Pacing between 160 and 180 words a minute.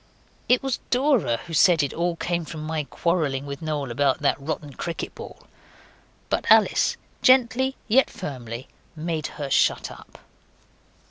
No: average, 145 wpm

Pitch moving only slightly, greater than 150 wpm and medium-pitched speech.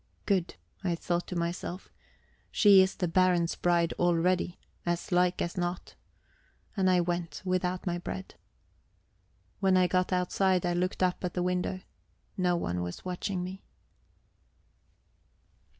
No: narrow, 1.0 semitones; slow, 135 wpm; medium, 180 Hz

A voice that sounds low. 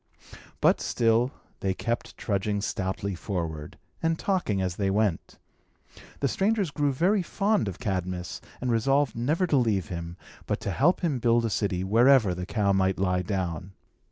Yes: low, 105 Hz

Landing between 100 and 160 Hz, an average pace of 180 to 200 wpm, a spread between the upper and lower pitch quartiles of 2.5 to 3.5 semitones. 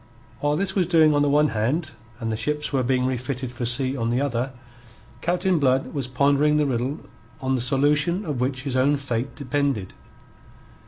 Yes: medium, 140 Hz; average, 190 wpm; average, 2.8 semitones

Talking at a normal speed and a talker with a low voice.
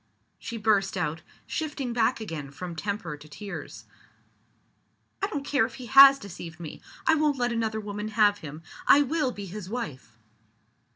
No: average, 165 wpm; high, 215 Hz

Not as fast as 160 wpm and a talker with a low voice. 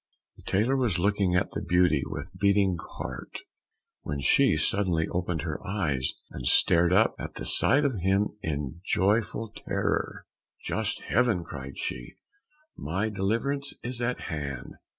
Yes: average, 145 wpm; very low, 95 Hz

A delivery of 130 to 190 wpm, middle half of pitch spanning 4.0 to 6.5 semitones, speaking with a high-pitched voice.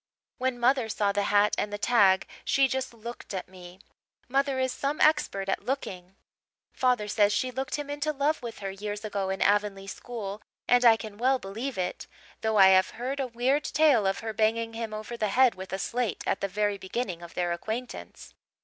No: fast, 205 wpm; average, 4.4 semitones; high, 220 Hz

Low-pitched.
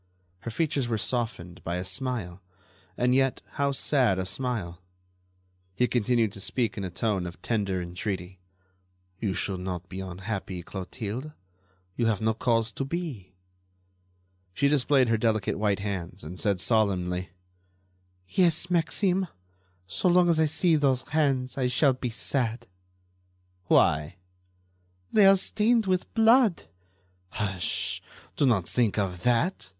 Yes: low, 115 Hz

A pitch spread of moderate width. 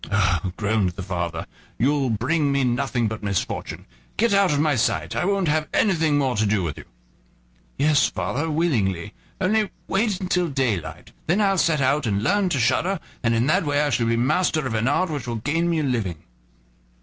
No: wide, 7.3 semitones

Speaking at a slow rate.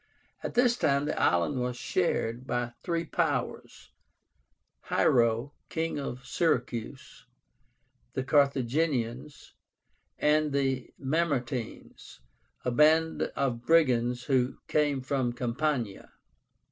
Yes: slow, 95 wpm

